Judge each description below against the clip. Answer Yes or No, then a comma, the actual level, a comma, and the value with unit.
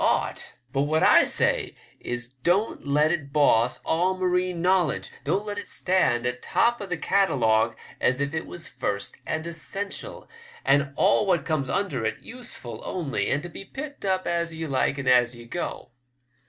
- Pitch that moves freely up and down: Yes, wide, 6.1 semitones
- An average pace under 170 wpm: No, average, 175 wpm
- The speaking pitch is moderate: Yes, medium, 160 Hz